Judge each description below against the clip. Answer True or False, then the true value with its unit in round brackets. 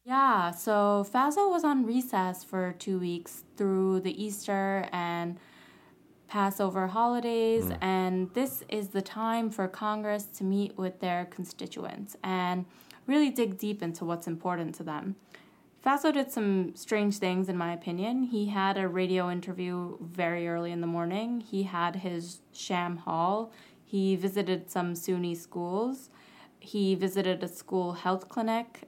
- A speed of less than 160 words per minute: True (145 wpm)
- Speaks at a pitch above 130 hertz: True (190 Hz)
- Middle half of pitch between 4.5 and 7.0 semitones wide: False (3.1 semitones)